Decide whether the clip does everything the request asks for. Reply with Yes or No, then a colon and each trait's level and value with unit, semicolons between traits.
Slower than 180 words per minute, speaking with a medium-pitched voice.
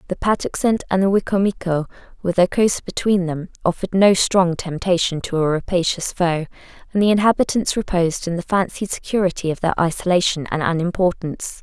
Yes: average, 160 wpm; medium, 180 Hz